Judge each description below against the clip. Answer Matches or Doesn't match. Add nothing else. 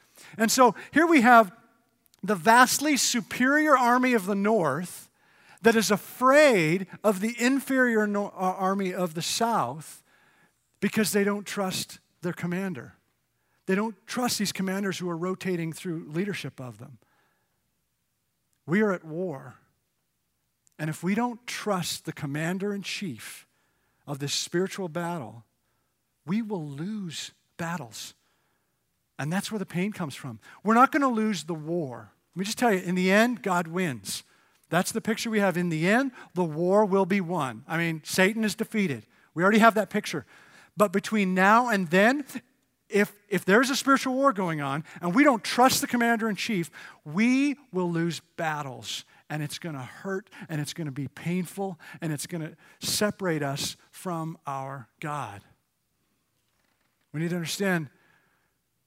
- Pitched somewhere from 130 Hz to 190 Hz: Matches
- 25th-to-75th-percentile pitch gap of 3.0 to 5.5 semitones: Matches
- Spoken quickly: Doesn't match